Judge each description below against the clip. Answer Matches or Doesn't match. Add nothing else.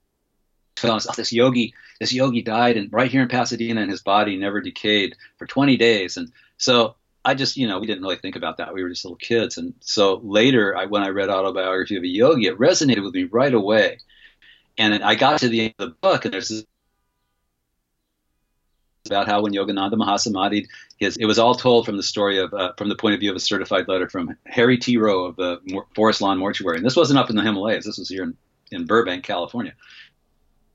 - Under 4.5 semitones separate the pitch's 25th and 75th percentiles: Matches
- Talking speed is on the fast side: Matches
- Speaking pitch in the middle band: Doesn't match